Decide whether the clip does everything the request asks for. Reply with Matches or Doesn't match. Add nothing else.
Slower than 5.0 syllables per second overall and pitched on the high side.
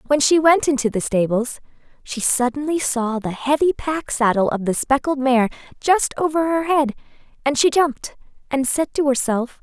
Matches